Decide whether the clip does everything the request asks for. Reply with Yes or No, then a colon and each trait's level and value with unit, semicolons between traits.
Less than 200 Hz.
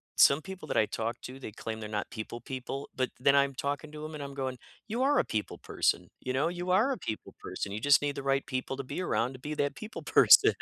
Yes: medium, 140 Hz